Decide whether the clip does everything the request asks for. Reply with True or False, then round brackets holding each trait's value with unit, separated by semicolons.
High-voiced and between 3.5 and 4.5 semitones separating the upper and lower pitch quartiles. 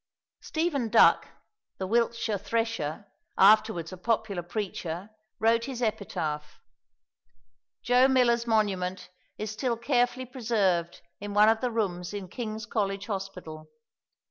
True (215 Hz; 3.9 semitones)